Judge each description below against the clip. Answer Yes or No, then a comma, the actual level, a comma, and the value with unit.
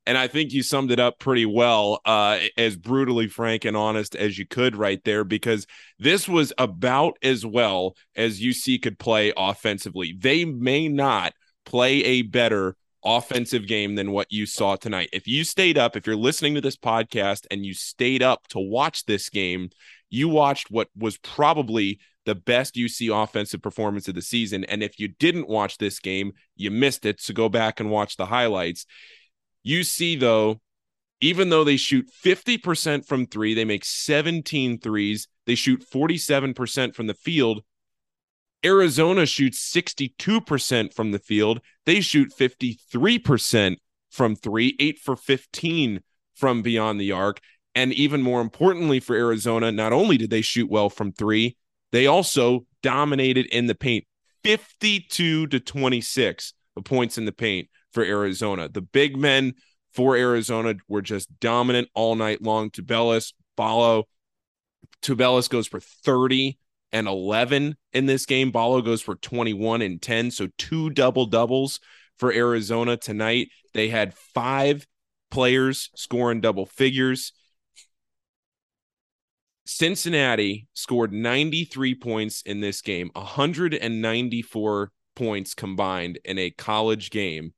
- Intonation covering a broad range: No, average, 4.0 semitones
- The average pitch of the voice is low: Yes, low, 115 Hz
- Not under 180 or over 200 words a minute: No, average, 145 wpm